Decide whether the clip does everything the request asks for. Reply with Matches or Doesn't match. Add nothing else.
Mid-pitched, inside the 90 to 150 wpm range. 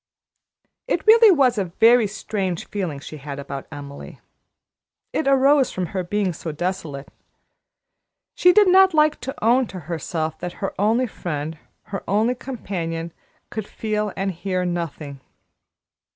Doesn't match